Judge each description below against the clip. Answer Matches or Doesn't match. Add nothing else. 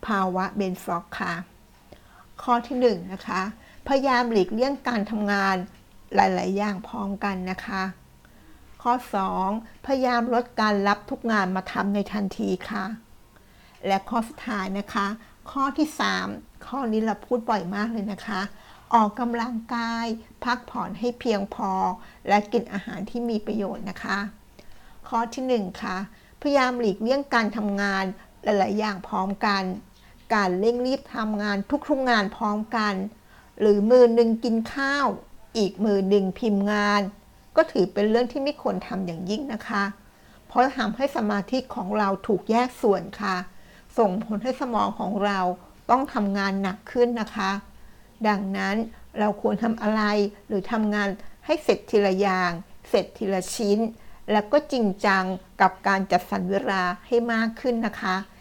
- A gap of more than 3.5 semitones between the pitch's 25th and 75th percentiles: Doesn't match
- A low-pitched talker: Doesn't match